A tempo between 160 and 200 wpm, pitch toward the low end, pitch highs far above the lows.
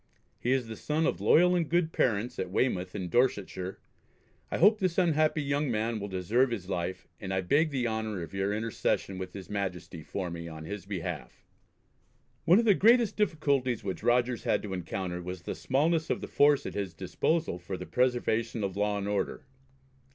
Yes: average, 195 wpm; low, 110 Hz; wide, 7.3 semitones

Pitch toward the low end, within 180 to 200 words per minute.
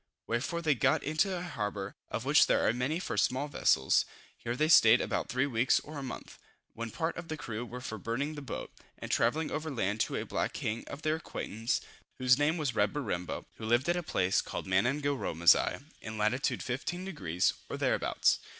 Yes: low, 130 Hz; average, 195 wpm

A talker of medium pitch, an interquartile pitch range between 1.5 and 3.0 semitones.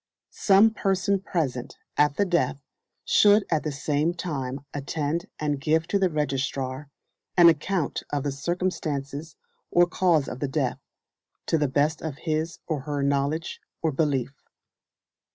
No: medium, 150 Hz; average, 3.5 semitones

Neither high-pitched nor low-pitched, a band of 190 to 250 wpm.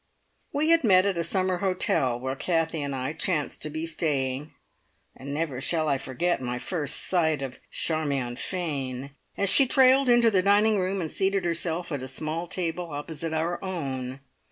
No: medium, 165 Hz; average, 180 wpm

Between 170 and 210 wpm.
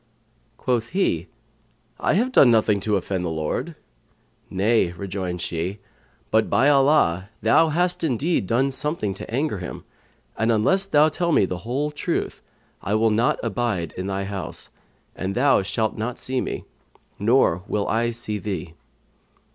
No: average, 155 wpm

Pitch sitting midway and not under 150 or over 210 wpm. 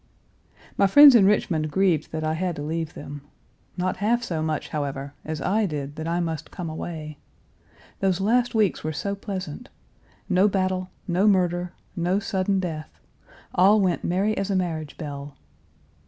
Yes: medium, 175 Hz; average, 165 wpm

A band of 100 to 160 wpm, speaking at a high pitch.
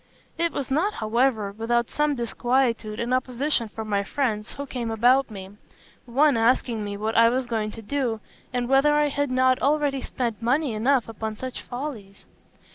No: average, 175 wpm; high, 245 Hz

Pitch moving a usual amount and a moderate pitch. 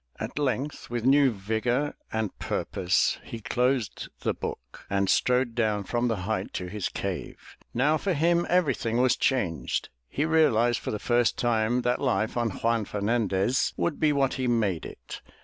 No: average, 3.8 semitones; low, 120 Hz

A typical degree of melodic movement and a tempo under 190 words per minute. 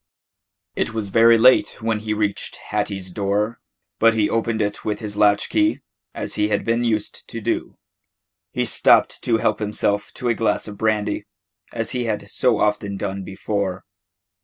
No: narrow, 1.8 semitones; average, 170 wpm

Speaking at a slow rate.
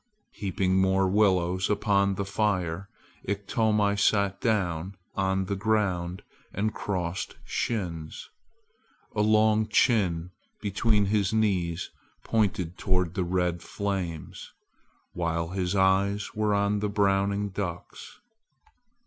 Yes: slow, 105 wpm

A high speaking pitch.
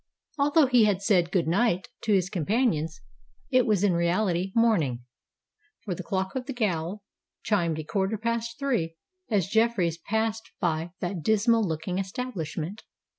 Yes: high, 195 Hz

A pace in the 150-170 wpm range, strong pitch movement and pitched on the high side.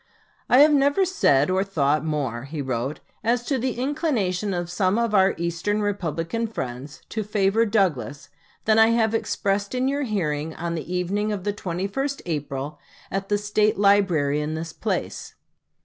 Yes: average, 165 wpm; wide, 5.8 semitones; high, 195 Hz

